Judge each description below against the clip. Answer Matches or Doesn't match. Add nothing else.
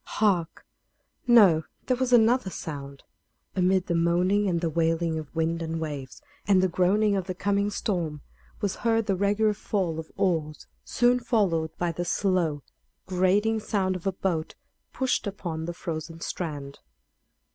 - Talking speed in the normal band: Matches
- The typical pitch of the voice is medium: Matches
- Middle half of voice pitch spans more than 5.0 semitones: Doesn't match